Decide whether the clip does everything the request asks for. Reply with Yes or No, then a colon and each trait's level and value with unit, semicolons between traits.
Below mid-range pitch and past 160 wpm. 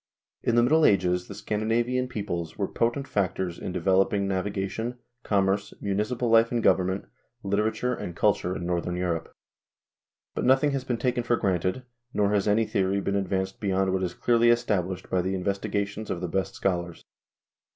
Yes: low, 100 Hz; average, 170 wpm